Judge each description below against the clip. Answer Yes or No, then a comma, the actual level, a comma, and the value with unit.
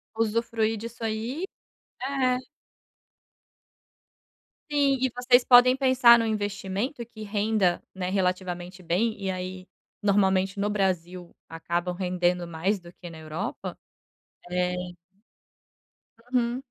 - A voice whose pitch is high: Yes, high, 200 Hz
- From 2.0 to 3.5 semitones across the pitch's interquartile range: No, average, 4.5 semitones